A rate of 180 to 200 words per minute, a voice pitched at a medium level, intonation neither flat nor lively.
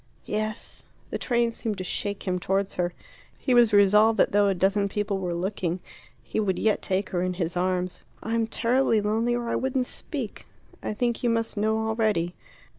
No: average, 190 wpm; high, 210 Hz; average, 3.3 semitones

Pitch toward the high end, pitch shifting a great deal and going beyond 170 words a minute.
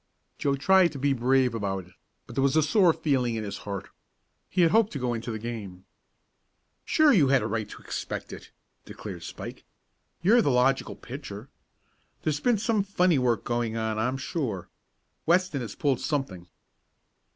No: low, 130 Hz; wide, 5.9 semitones; average, 180 wpm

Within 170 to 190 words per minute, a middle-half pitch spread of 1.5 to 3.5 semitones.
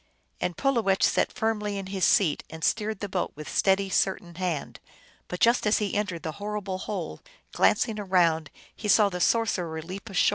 Yes: average, 180 wpm; average, 2.9 semitones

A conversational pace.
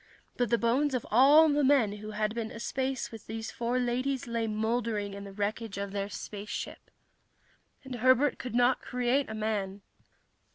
Yes: average, 170 wpm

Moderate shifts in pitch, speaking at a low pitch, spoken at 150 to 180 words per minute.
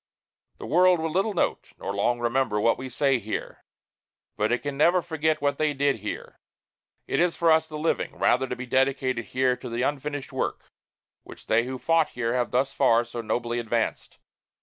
No: average, 4.5 semitones; low, 130 Hz; average, 195 wpm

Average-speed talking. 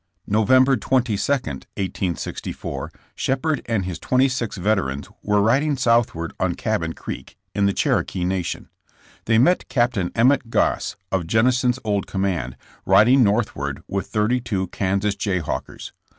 No: slow, 130 wpm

